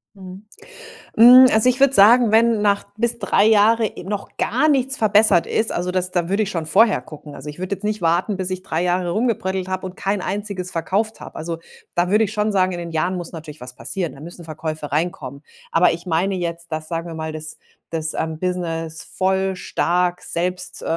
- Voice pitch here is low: No, medium, 185 Hz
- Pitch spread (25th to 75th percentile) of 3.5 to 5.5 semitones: Yes, average, 3.9 semitones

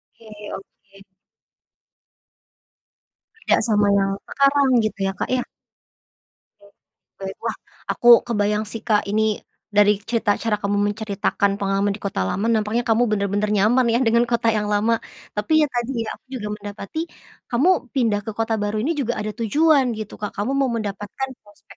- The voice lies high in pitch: Yes, high, 215 Hz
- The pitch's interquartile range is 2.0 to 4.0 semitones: Yes, narrow, 2.5 semitones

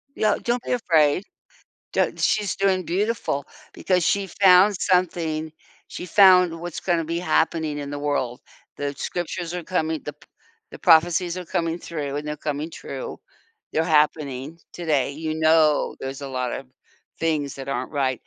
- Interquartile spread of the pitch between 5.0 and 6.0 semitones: No, average, 3.6 semitones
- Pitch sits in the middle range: Yes, medium, 160 Hz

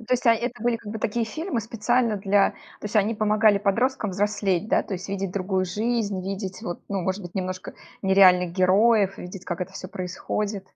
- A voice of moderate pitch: No, high, 200 Hz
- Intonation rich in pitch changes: No, average, 2.8 semitones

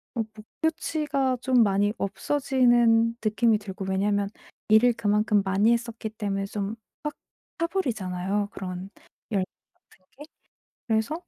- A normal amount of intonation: Yes, average, 3.5 semitones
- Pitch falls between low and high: No, high, 215 Hz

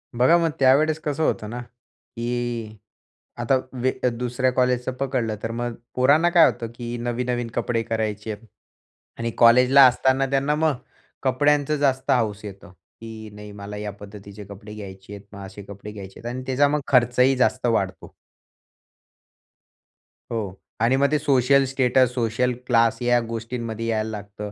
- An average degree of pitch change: Yes, average, 3.5 semitones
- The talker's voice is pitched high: No, low, 120 Hz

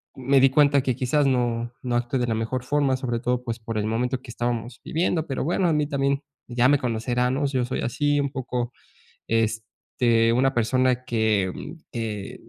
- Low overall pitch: Yes, low, 125 Hz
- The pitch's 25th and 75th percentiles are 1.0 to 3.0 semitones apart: Yes, narrow, 2.6 semitones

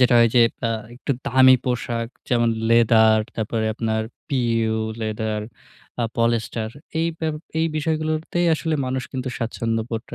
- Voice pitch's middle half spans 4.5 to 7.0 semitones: No, average, 2.8 semitones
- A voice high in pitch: No, low, 115 Hz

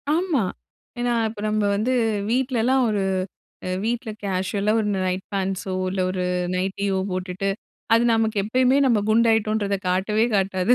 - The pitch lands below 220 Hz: Yes, high, 210 Hz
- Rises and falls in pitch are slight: No, average, 3.3 semitones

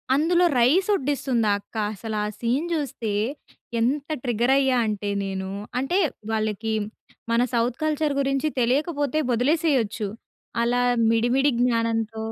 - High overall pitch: Yes, high, 245 Hz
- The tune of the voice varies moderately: Yes, average, 4.3 semitones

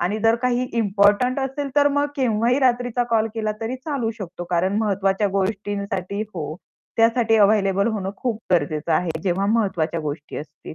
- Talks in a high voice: Yes, high, 210 Hz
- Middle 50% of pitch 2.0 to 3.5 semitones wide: No, average, 3.9 semitones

